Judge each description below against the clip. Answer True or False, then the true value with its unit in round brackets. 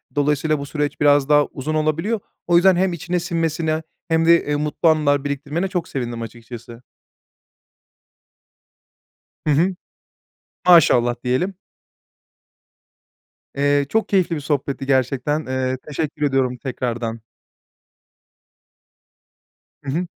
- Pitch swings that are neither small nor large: True (3.8 semitones)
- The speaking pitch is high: False (145 Hz)